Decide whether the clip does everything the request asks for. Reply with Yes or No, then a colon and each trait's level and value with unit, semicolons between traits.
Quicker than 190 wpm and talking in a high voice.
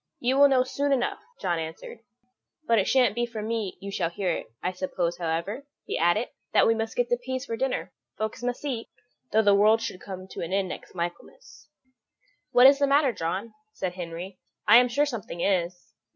Yes: fast, 205 wpm; high, 215 Hz